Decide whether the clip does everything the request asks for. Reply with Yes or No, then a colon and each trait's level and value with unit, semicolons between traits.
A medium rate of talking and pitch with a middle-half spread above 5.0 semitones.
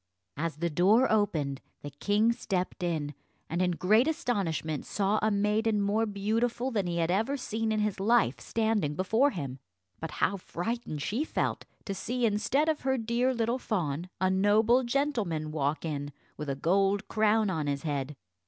Yes: average, 170 wpm; wide, 5.6 semitones